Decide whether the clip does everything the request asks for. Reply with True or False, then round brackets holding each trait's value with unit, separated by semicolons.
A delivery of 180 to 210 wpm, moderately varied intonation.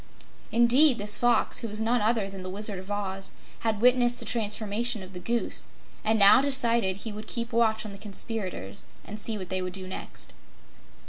True (195 wpm; 3.0 semitones)